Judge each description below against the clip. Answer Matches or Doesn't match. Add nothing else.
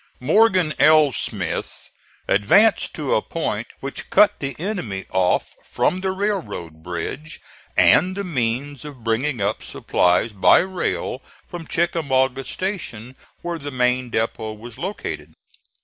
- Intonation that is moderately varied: Doesn't match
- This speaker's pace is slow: Matches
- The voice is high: Doesn't match